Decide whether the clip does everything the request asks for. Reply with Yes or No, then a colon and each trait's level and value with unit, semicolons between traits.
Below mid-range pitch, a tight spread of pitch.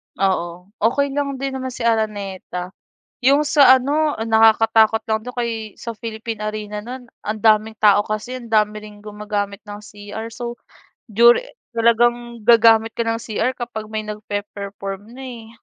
No: high, 220 Hz; narrow, 2.3 semitones